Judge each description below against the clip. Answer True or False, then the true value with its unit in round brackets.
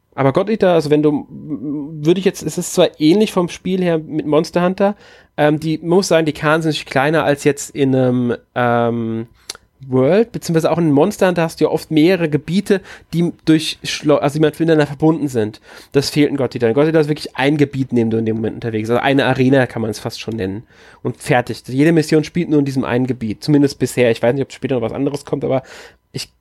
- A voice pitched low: False (145 Hz)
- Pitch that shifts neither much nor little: True (3.9 semitones)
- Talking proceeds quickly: True (235 wpm)